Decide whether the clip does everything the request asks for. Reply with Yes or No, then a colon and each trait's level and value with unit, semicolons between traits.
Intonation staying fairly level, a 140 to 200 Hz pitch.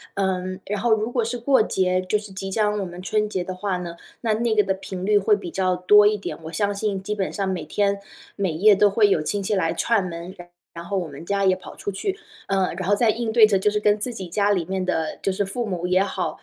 Yes: narrow, 2.3 semitones; high, 195 Hz